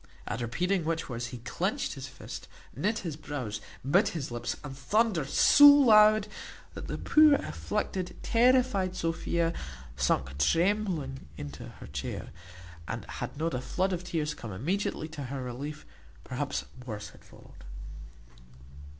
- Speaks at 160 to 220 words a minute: No, average, 140 wpm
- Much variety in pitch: Yes, wide, 8.0 semitones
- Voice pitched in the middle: Yes, medium, 160 Hz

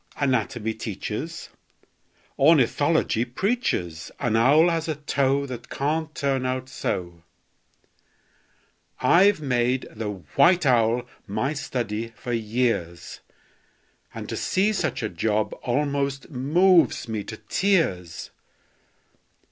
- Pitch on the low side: Yes, low, 130 Hz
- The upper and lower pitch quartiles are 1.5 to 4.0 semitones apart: No, average, 5.3 semitones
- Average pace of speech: No, slow, 105 wpm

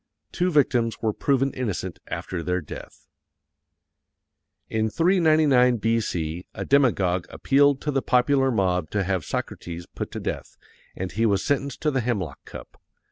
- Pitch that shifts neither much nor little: No, wide, 6.9 semitones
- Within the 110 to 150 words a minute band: Yes, average, 145 wpm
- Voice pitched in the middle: No, low, 115 Hz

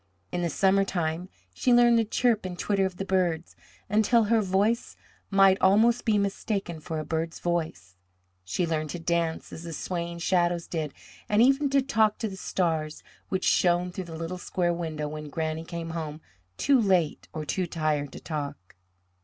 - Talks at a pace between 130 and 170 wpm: No, average, 180 wpm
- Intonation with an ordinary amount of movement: Yes, average, 3.6 semitones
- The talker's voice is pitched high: No, medium, 175 Hz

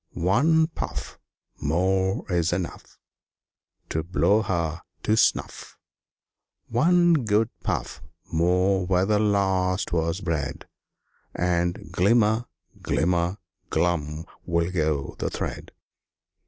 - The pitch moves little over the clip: No, average, 3.5 semitones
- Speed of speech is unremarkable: No, slow, 95 wpm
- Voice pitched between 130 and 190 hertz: No, very low, 90 Hz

